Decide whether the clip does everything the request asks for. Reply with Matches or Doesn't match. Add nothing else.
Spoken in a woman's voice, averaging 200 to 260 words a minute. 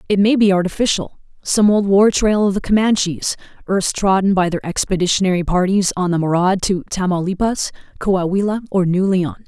Doesn't match